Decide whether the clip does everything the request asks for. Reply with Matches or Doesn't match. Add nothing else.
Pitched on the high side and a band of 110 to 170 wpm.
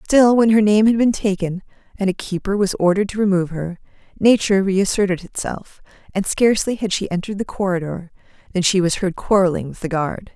Doesn't match